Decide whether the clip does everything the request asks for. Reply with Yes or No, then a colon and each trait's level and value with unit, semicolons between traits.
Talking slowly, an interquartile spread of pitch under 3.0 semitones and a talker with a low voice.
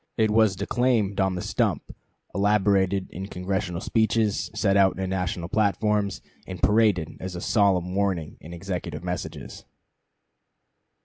Yes: slow, 130 wpm; narrow, 2.4 semitones; very low, 95 Hz